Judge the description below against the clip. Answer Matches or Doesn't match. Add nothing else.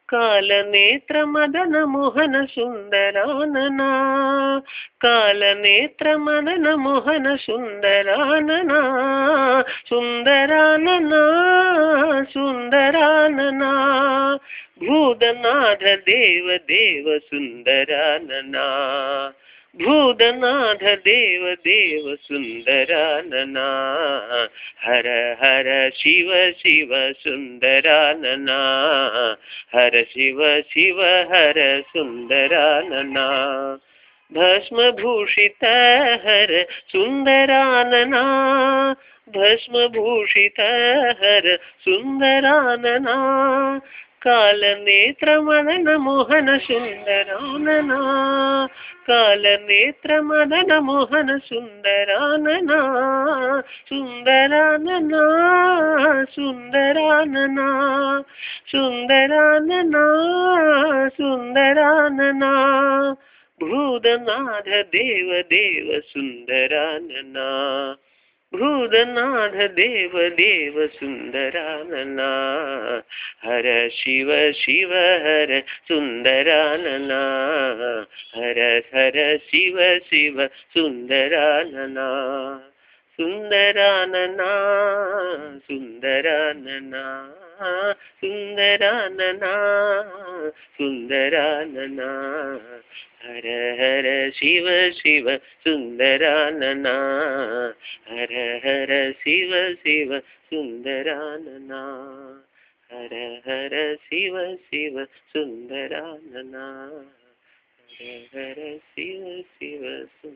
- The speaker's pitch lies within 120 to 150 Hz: Doesn't match